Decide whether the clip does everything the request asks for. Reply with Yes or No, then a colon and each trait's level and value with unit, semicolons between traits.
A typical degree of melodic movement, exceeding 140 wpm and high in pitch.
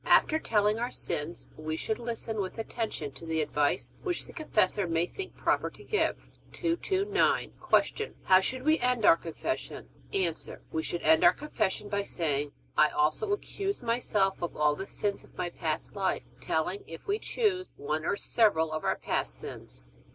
No: wide, 7.7 semitones; average, 175 wpm; high, 195 Hz